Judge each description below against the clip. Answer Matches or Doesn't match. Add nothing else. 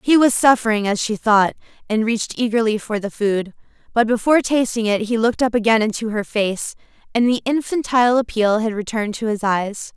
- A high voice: Matches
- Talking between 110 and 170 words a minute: Doesn't match